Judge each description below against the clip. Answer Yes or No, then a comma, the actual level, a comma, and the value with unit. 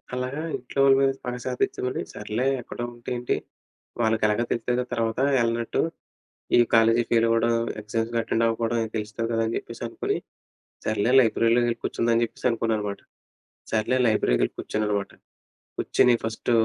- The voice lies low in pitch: Yes, low, 115 Hz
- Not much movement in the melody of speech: Yes, narrow, 1.2 semitones